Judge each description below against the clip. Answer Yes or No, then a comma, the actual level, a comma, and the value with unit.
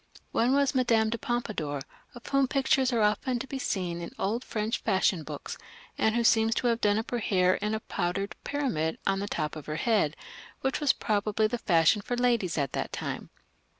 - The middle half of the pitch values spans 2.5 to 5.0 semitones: Yes, average, 4.6 semitones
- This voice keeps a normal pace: No, fast, 210 wpm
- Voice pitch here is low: No, high, 220 Hz